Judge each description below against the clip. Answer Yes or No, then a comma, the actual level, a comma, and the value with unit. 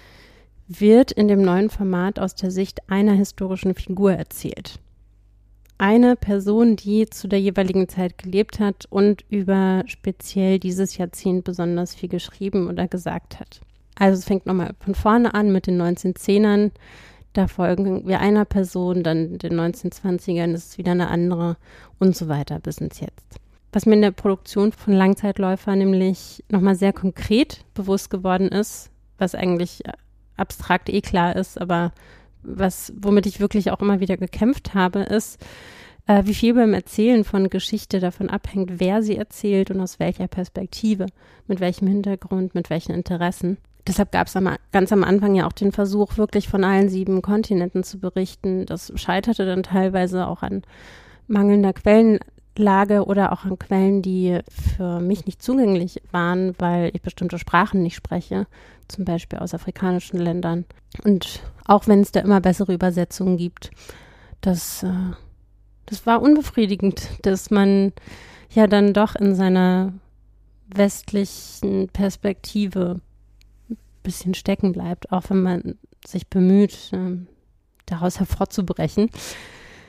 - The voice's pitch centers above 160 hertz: Yes, high, 190 Hz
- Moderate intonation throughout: No, narrow, 1.9 semitones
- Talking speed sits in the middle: Yes, average, 145 wpm